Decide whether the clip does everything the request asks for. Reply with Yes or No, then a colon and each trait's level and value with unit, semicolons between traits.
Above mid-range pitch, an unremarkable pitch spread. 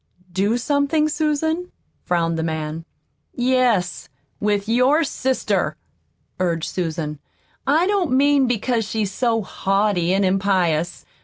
No: high, 215 Hz; wide, 7.6 semitones